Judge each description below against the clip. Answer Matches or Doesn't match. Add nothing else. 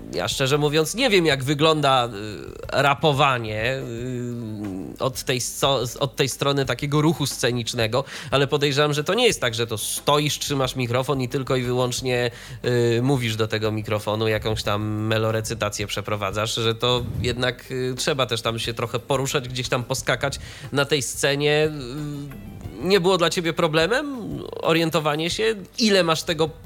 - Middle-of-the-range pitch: Doesn't match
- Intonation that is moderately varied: Matches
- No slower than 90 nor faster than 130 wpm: Doesn't match